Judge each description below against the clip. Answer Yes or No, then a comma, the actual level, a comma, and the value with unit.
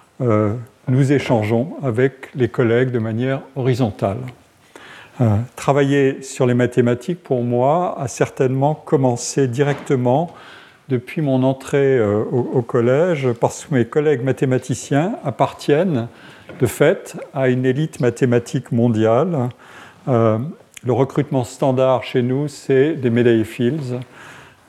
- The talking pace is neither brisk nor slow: No, slow, 120 wpm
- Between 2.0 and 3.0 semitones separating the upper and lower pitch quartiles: Yes, narrow, 2.4 semitones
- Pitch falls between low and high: No, low, 130 Hz